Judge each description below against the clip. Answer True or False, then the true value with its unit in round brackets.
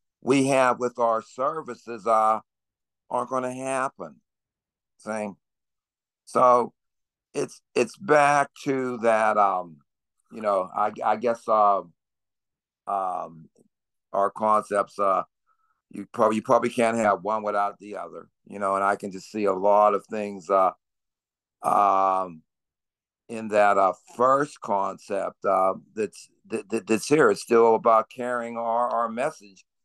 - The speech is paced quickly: False (140 wpm)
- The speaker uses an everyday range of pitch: True (3.2 semitones)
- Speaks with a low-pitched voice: True (110 Hz)